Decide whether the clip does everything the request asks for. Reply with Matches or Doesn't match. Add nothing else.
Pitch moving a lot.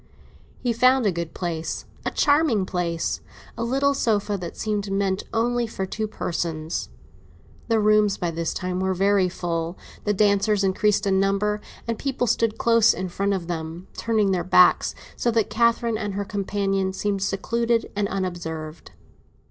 Doesn't match